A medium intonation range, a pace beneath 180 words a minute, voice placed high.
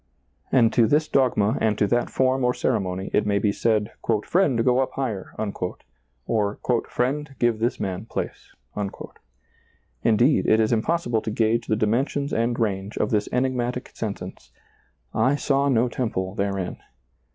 No: average, 3.5 semitones; average, 160 wpm; low, 115 Hz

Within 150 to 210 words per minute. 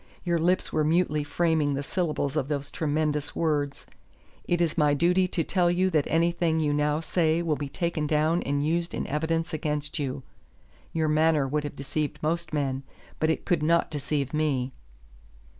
Yes: average, 175 wpm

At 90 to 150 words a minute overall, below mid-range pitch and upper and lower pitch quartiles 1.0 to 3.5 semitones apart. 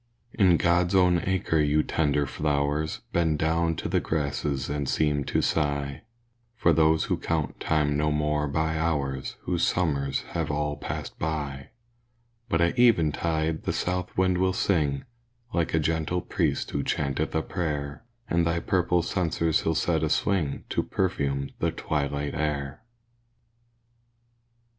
Yes: average, 145 wpm; very low, 80 Hz; average, 2.7 semitones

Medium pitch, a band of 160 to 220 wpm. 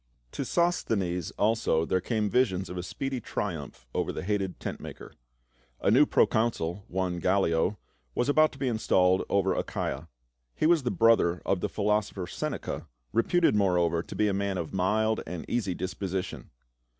No: low, 100 Hz; average, 175 wpm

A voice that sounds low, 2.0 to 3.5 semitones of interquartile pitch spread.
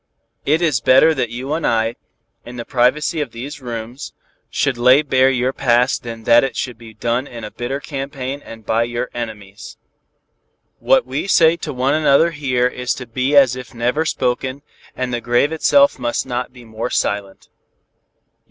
Yes: low, 125 Hz; average, 3.0 semitones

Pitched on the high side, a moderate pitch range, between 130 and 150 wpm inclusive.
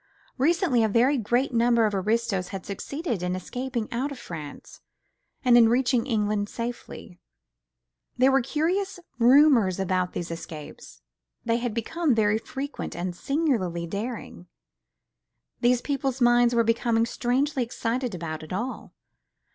Yes: high, 235 Hz; average, 4.7 semitones; slow, 135 wpm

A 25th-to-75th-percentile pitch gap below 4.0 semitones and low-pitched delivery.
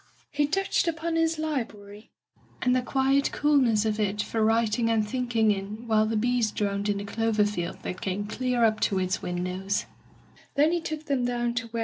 No: average, 3.6 semitones; high, 220 Hz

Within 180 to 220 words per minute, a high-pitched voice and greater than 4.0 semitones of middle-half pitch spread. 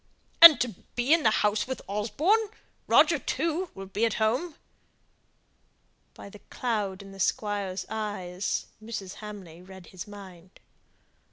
No: average, 140 wpm; high, 210 Hz; average, 4.6 semitones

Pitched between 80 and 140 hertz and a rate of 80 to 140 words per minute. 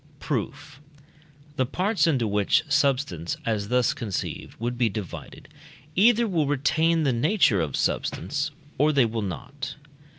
Yes: low, 135 Hz; slow, 135 wpm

